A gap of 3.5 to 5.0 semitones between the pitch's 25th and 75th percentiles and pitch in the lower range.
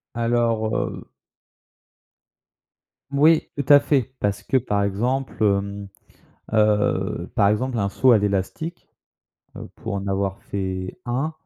Yes: average, 4.5 semitones; low, 110 Hz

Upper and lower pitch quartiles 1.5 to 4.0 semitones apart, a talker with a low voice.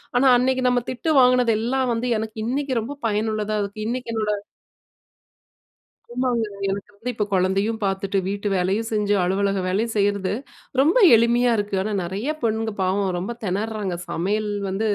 No: average, 3.2 semitones; high, 215 Hz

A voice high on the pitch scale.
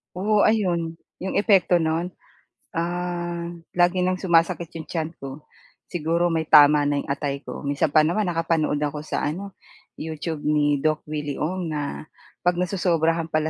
No: medium, 165 Hz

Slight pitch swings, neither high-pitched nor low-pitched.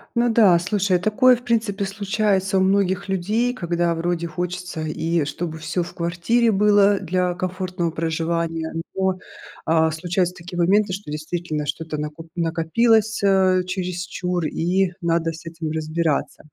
No: average, 3.0 semitones; medium, 180 Hz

